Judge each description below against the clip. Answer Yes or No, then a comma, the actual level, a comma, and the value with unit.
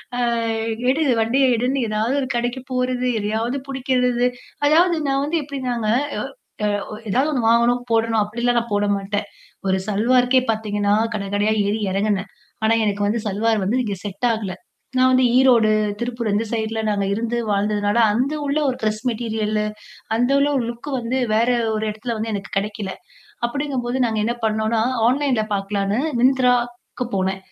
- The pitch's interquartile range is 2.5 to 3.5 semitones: Yes, average, 3.0 semitones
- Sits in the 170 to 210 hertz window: No, high, 230 Hz